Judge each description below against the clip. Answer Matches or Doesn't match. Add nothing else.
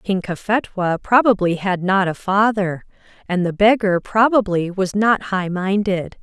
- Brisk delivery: Doesn't match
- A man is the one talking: Doesn't match